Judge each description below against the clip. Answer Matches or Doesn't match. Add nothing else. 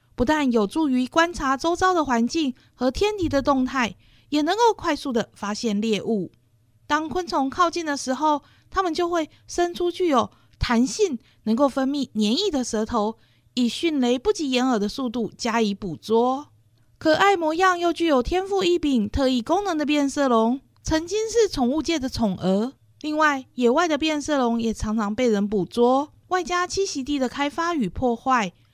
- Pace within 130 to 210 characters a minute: Doesn't match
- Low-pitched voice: Doesn't match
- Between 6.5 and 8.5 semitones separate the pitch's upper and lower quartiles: Doesn't match